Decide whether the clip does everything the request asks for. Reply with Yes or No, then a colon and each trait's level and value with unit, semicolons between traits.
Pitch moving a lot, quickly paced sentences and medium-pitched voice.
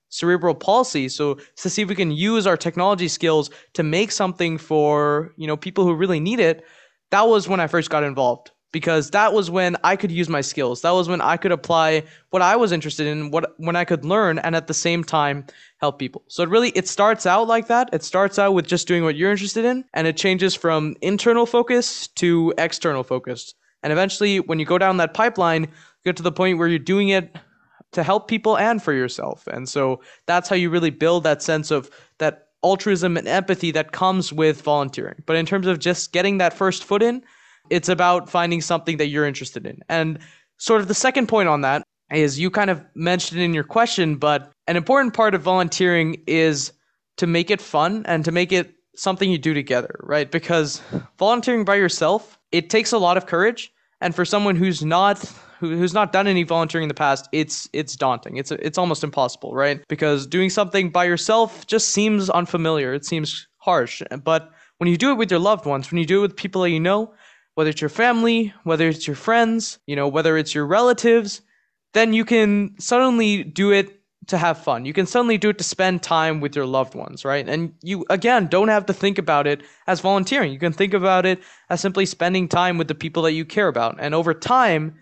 No: average, 4.0 semitones; fast, 220 wpm; medium, 175 Hz